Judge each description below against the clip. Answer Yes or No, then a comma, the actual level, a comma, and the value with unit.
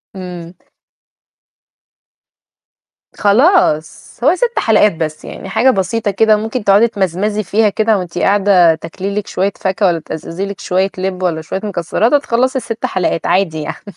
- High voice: Yes, high, 195 Hz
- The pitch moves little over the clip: No, average, 3.5 semitones